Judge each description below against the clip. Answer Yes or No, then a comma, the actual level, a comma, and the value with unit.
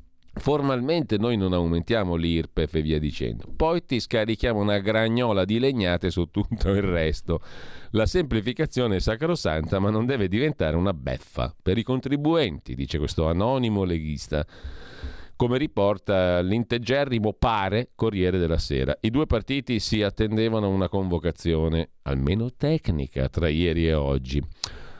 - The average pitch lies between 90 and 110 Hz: Yes, low, 100 Hz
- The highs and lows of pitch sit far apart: Yes, wide, 6.1 semitones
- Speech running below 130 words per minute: No, average, 135 wpm